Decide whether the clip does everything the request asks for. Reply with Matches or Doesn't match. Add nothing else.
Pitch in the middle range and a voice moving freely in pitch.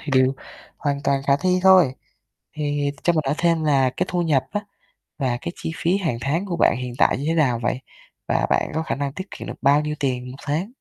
Doesn't match